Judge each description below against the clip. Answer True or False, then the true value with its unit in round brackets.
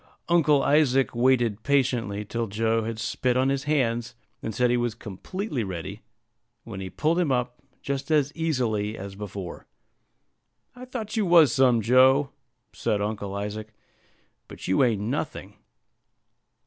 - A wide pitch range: False (4.8 semitones)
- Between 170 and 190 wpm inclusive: False (145 wpm)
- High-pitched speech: False (120 Hz)